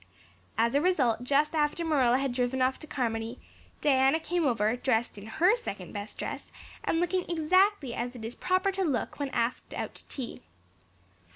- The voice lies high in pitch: Yes, very high, 270 Hz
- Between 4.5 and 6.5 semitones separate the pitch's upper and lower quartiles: Yes, wide, 5.4 semitones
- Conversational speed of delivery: Yes, average, 180 wpm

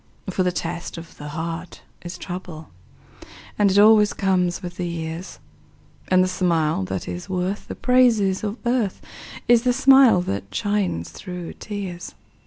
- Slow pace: No, average, 155 wpm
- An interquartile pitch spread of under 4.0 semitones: Yes, average, 3.5 semitones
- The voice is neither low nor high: Yes, medium, 180 Hz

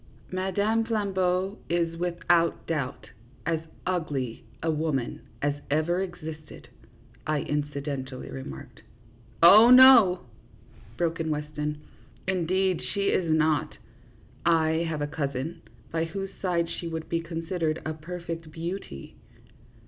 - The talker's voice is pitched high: No, medium, 165 Hz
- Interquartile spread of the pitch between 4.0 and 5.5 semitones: No, average, 3.0 semitones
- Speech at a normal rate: No, slow, 125 wpm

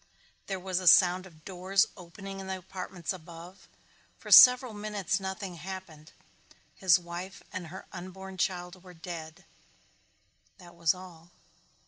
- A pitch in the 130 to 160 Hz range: No, medium, 185 Hz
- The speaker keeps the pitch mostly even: Yes, narrow, 1.8 semitones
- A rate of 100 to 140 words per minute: Yes, slow, 135 wpm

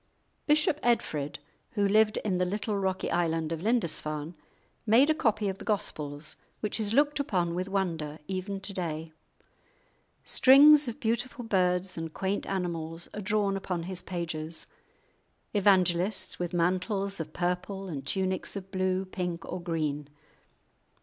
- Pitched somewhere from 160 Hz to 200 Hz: Yes, medium, 185 Hz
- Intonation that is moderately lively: Yes, average, 3.6 semitones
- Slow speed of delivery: No, average, 145 wpm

